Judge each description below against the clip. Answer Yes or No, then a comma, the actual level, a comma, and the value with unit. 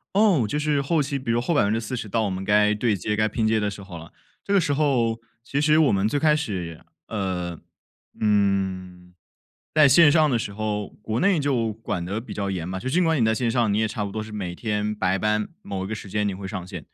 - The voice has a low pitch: Yes, low, 110 Hz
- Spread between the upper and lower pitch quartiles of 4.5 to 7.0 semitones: Yes, average, 5.1 semitones